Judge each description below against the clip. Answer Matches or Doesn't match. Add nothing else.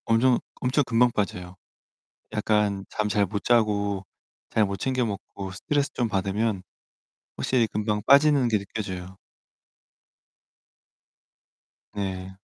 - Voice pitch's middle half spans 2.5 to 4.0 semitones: Matches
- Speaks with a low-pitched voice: Matches